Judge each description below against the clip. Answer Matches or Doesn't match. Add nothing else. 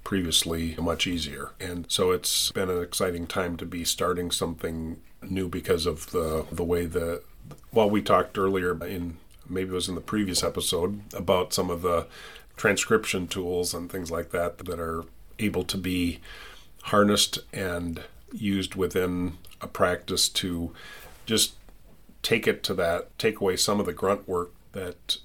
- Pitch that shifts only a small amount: Matches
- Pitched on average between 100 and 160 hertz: Doesn't match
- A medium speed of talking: Matches